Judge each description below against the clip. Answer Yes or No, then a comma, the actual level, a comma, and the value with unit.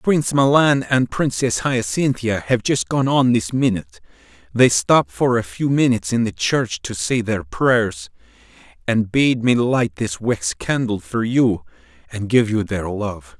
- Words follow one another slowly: No, average, 170 wpm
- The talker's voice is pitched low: Yes, low, 110 Hz